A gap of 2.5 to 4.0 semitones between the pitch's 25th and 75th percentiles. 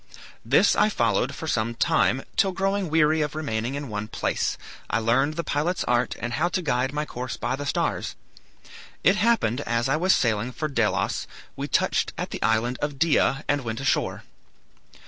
No: average, 4.8 semitones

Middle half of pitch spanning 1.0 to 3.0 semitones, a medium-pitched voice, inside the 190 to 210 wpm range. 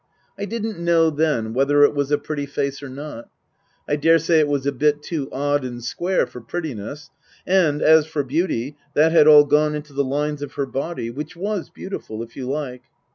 Yes: narrow, 2.5 semitones; medium, 145 Hz; average, 200 wpm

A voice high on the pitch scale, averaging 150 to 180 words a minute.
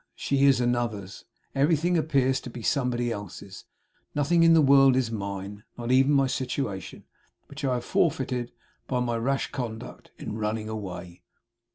No: low, 125 Hz; average, 155 wpm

